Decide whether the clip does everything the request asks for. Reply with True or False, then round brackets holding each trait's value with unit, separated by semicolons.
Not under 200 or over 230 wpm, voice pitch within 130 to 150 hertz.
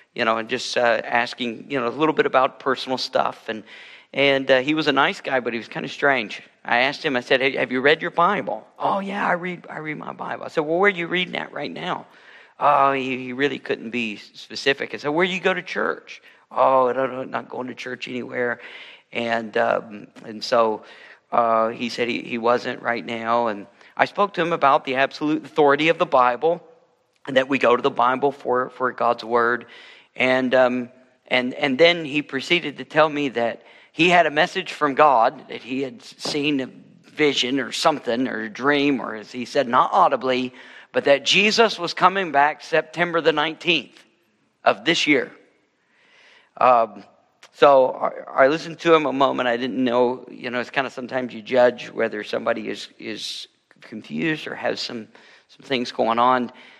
True (205 wpm; 135 Hz)